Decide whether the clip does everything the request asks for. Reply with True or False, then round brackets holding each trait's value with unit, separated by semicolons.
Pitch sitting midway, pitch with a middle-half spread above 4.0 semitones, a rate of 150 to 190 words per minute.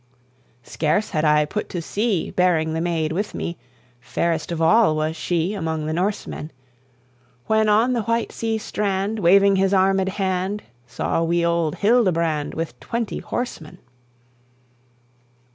False (180 Hz; 4.5 semitones; 140 wpm)